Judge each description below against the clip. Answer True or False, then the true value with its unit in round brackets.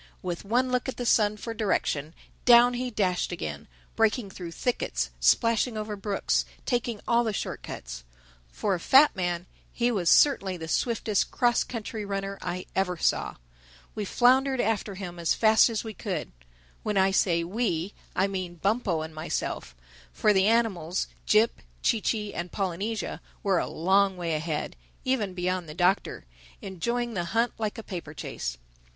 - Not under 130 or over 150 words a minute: False (160 wpm)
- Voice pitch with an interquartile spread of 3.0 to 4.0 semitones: False (4.5 semitones)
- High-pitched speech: True (200 Hz)